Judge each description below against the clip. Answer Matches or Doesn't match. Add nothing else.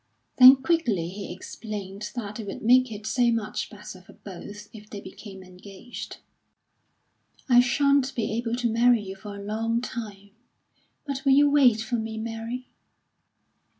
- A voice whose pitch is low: Doesn't match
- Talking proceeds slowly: Doesn't match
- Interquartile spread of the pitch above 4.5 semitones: Doesn't match